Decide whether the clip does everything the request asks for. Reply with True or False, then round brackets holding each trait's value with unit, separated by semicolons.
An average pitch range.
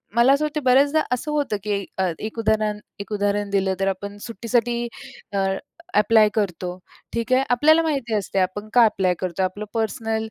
True (3.5 semitones)